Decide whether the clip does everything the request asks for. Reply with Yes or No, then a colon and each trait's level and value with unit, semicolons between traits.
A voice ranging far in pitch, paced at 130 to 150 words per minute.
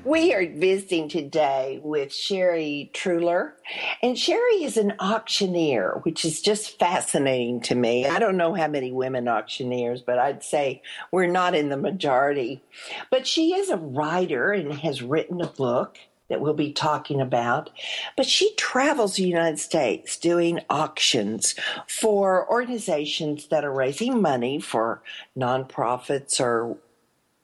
Yes: wide, 7.0 semitones; average, 140 wpm